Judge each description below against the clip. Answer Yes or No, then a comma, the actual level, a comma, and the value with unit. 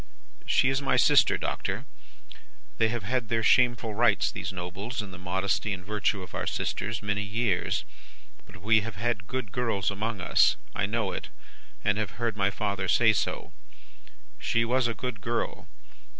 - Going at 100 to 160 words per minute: No, average, 170 wpm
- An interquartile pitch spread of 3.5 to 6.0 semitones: No, average, 3.0 semitones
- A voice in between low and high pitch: No, low, 105 Hz